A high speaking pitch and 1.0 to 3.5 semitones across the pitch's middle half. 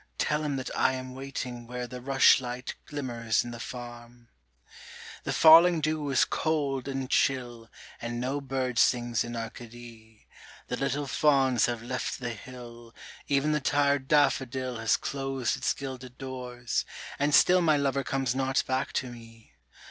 No: low, 130 Hz; narrow, 2.4 semitones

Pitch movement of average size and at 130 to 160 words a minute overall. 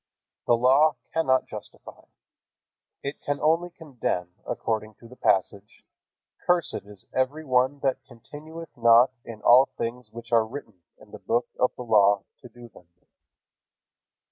Yes: average, 4.2 semitones; average, 140 wpm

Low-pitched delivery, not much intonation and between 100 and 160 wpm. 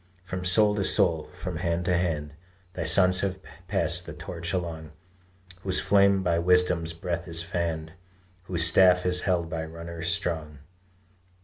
Yes: very low, 85 Hz; narrow, 1.7 semitones; average, 150 wpm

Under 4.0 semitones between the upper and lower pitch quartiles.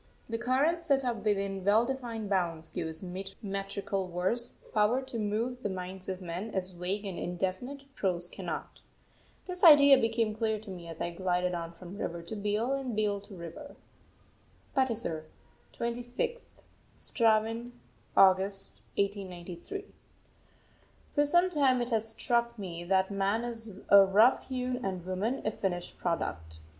No: average, 4.5 semitones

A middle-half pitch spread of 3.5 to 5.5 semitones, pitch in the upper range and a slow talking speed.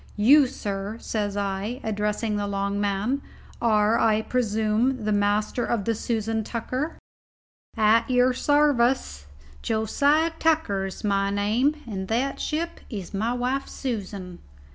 Yes: average, 3.8 semitones; high, 220 Hz; slow, 130 wpm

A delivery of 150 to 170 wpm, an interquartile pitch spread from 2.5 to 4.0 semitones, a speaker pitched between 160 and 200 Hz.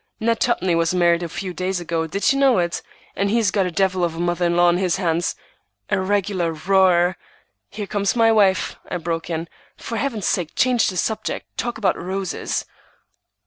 No: average, 195 wpm; average, 2.9 semitones; medium, 185 Hz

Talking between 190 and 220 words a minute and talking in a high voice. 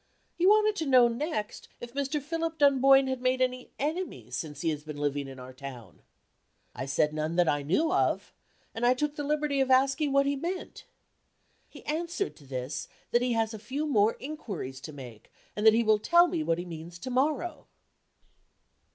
Yes: average, 195 wpm; very high, 250 Hz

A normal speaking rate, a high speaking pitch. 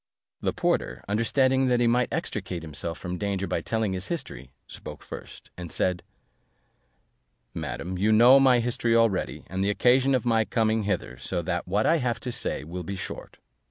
No: average, 185 wpm; low, 105 Hz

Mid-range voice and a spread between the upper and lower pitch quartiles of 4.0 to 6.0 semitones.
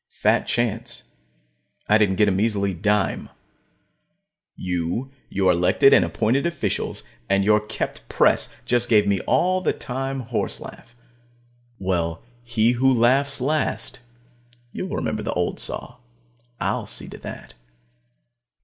No: low, 110 Hz; average, 4.8 semitones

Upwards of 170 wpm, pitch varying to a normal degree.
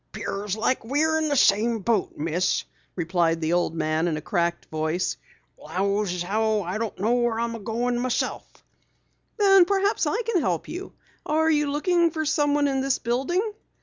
No: average, 185 wpm; wide, 8.7 semitones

